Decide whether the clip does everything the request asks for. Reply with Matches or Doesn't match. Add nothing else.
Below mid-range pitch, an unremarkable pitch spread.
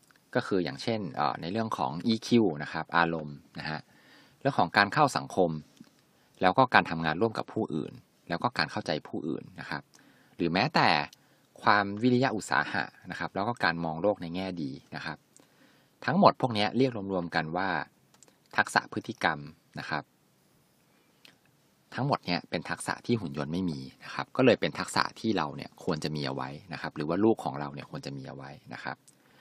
Doesn't match